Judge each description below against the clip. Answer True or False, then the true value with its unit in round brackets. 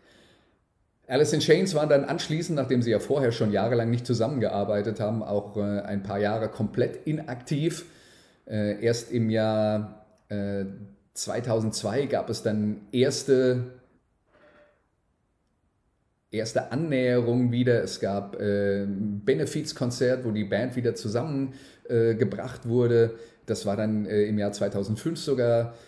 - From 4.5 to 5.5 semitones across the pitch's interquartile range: False (3.6 semitones)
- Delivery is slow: True (115 wpm)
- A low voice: True (115 Hz)